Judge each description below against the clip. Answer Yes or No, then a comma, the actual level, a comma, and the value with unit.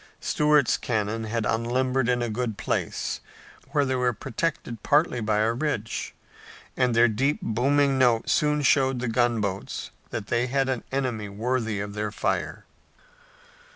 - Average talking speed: Yes, average, 150 wpm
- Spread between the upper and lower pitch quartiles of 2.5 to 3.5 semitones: Yes, average, 3.1 semitones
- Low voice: Yes, low, 120 Hz